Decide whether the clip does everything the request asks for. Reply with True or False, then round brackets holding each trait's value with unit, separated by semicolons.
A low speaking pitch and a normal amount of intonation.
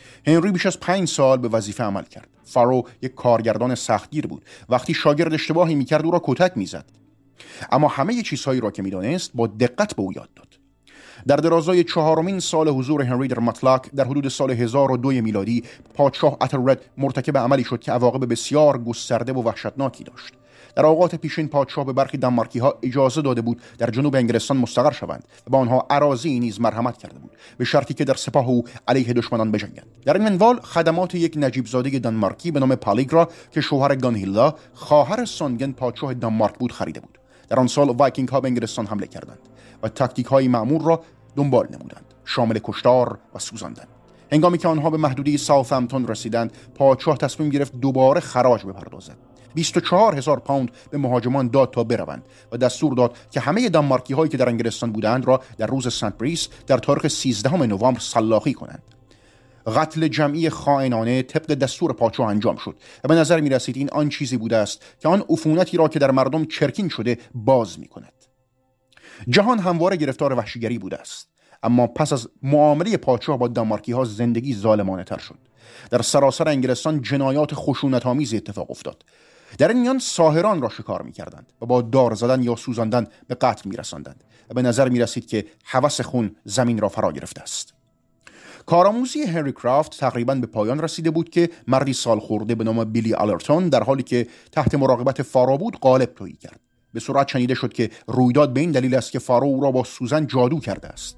True (130 Hz; 3.7 semitones)